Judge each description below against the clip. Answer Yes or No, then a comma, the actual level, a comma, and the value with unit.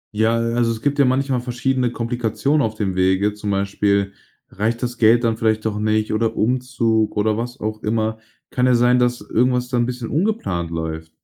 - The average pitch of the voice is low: Yes, low, 115 Hz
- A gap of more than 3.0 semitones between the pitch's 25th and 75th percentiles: No, average, 2.7 semitones